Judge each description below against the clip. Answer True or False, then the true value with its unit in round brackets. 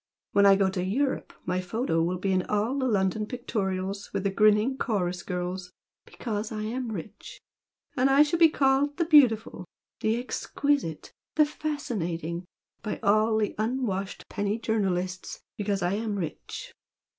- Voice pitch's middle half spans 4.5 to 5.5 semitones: True (5.0 semitones)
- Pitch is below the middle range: False (210 Hz)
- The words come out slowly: False (155 wpm)